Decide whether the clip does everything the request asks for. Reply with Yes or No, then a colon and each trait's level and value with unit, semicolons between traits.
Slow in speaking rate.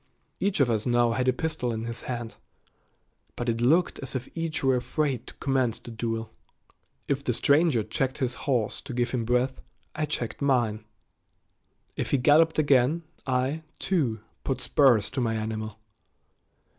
No: average, 165 wpm